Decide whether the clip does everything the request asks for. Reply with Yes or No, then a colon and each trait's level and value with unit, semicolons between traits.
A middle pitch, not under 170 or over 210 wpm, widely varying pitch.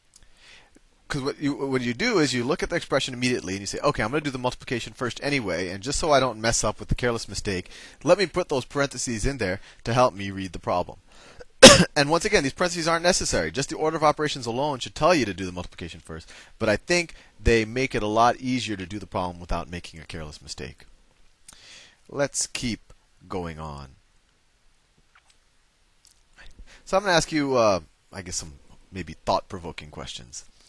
No: low, 115 Hz; fast, 205 wpm; wide, 7.4 semitones